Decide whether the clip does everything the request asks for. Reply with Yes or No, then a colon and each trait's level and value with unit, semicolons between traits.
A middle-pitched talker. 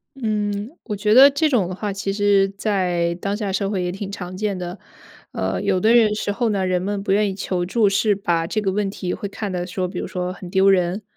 No: high, 195 Hz